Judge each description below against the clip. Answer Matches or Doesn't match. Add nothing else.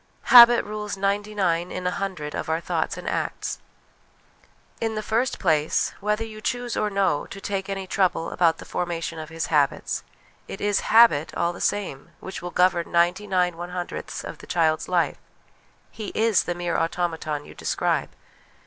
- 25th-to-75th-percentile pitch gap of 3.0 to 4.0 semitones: Matches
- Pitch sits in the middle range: Matches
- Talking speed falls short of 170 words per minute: Doesn't match